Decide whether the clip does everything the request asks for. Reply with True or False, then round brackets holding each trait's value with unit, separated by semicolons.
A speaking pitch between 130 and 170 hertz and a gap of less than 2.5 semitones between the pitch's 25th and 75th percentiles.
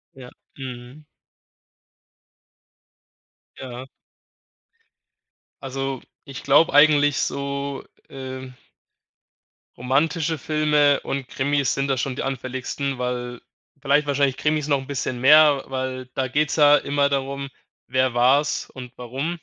True (135 Hz; 1.9 semitones)